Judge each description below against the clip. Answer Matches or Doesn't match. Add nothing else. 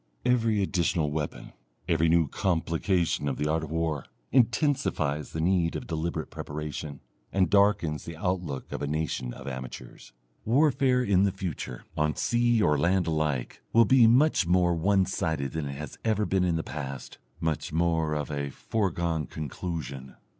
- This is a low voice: Matches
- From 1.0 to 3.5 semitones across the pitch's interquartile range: Doesn't match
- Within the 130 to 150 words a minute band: Doesn't match